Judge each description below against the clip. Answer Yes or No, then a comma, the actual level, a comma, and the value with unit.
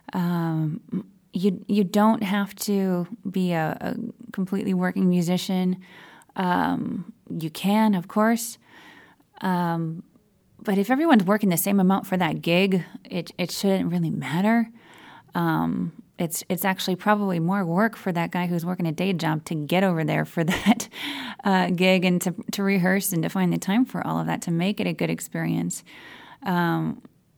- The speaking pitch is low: No, medium, 185 Hz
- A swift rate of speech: No, average, 165 wpm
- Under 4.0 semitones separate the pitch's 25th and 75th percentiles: Yes, average, 2.9 semitones